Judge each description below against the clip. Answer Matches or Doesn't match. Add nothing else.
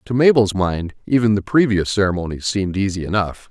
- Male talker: Matches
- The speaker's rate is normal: Matches